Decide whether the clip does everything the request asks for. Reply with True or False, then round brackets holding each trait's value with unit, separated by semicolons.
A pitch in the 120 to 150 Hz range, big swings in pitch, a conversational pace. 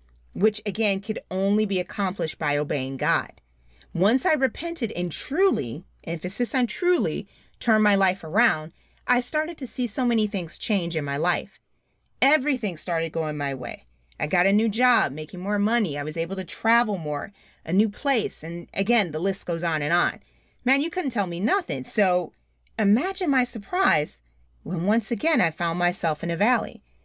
False (200 Hz; 6.3 semitones; 180 wpm)